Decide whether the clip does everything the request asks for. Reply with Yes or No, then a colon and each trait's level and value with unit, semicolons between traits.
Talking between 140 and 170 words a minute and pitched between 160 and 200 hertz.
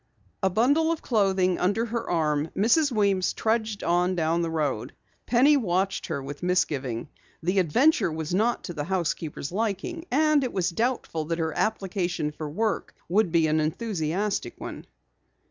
Yes: average, 160 wpm; medium, 185 Hz